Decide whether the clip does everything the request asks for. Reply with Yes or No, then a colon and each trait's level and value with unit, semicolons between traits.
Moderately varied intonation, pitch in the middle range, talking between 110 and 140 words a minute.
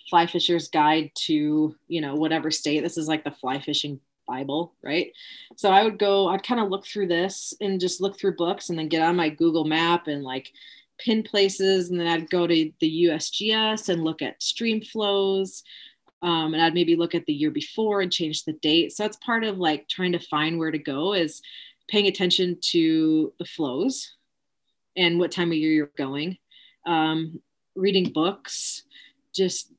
No: average, 3.8 semitones; medium, 175 Hz; average, 190 wpm